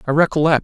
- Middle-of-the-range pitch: Yes, medium, 155 Hz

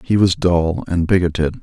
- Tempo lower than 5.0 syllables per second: Yes, 4.7 syllables/s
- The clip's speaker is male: Yes, male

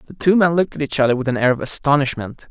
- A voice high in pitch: No, medium, 140 Hz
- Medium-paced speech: No, fast, 290 wpm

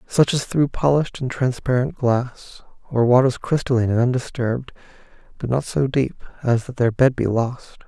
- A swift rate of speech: No, average, 170 wpm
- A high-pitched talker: No, low, 125 Hz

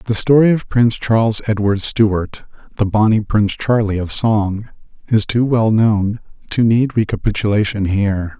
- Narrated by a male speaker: Yes, male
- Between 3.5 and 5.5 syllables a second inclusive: Yes, 4.7 syllables/s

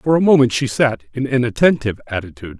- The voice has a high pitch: No, low, 125 Hz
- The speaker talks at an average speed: No, fast, 210 wpm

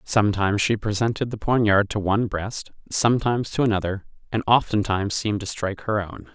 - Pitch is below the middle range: Yes, low, 105 Hz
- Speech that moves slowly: No, average, 170 wpm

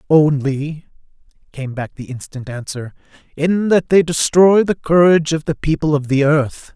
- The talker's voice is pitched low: No, medium, 150 Hz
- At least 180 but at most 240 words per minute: No, average, 160 wpm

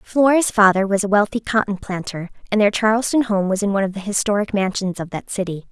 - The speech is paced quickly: Yes, fast, 220 wpm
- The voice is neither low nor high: No, high, 205 Hz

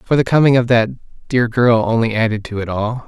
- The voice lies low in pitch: Yes, low, 115 Hz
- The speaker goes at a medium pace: No, fast, 235 wpm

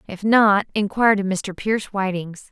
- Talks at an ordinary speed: Yes, average, 165 wpm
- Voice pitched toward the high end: Yes, high, 200 Hz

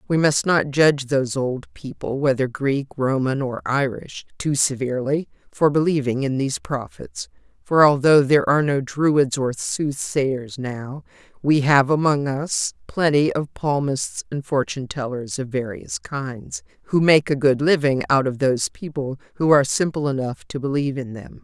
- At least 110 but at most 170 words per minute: Yes, average, 160 wpm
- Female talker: Yes, female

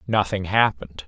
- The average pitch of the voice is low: Yes, very low, 95 Hz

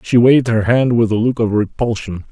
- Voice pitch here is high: No, low, 115 Hz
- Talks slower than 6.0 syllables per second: Yes, 5.5 syllables/s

